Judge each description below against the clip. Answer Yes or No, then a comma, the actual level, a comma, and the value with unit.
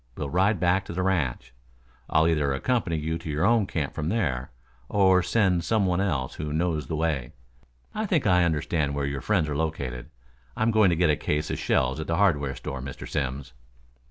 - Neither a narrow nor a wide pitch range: Yes, average, 4.7 semitones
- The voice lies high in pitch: No, very low, 80 Hz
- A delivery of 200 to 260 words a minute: Yes, fast, 205 wpm